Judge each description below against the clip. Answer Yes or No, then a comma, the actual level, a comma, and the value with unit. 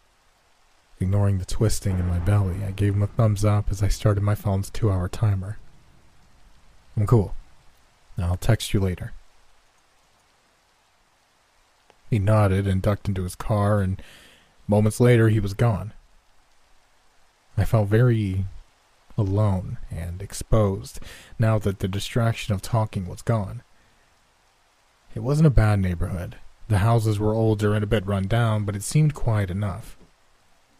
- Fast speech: No, average, 140 wpm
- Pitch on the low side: Yes, low, 105 Hz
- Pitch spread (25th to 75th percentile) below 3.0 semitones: Yes, narrow, 2.5 semitones